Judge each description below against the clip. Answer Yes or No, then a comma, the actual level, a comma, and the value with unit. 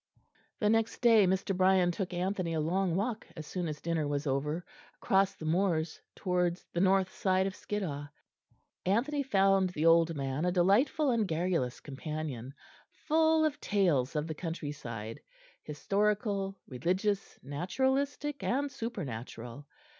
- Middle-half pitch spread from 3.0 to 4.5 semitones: No, average, 4.9 semitones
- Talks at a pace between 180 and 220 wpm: No, average, 140 wpm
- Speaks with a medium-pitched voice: Yes, medium, 180 Hz